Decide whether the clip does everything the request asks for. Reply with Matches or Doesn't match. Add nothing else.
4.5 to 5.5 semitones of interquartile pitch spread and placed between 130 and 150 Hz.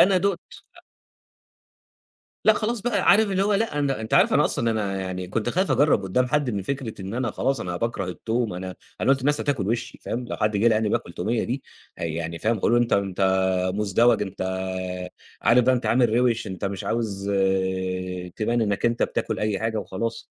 Doesn't match